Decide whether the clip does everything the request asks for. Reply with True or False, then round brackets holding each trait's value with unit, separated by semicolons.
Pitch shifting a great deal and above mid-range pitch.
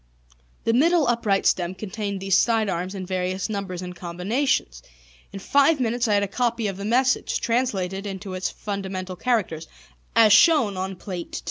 False (4.0 semitones; 200 Hz)